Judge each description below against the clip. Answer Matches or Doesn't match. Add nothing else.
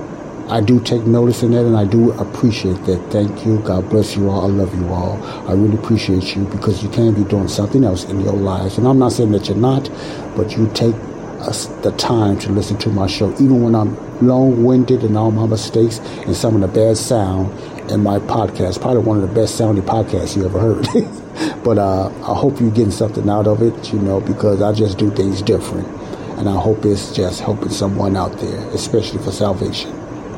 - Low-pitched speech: Matches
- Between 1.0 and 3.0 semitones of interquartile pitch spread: Matches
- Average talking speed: Doesn't match